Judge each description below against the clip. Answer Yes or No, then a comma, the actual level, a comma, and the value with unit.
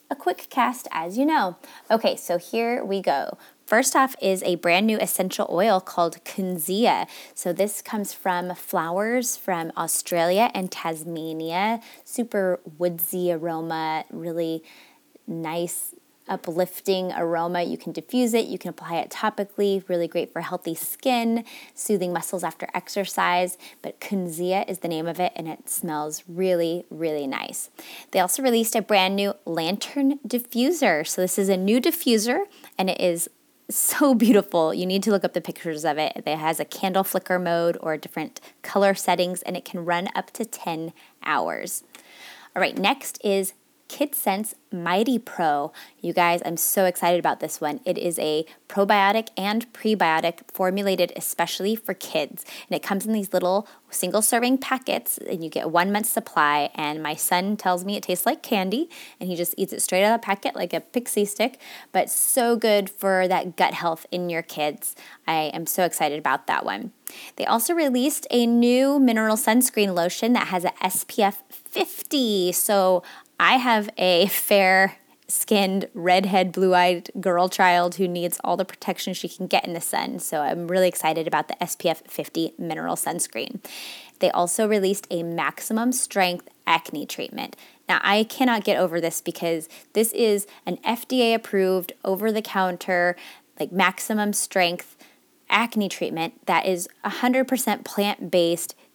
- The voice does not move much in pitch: No, average, 4.4 semitones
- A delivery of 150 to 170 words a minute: Yes, average, 165 wpm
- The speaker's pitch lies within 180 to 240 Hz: Yes, high, 190 Hz